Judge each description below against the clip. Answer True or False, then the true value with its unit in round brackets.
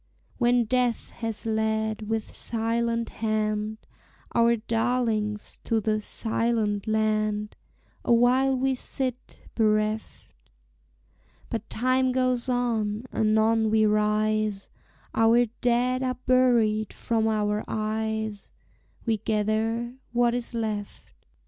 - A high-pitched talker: True (220 Hz)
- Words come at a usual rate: False (100 wpm)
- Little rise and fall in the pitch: True (1.9 semitones)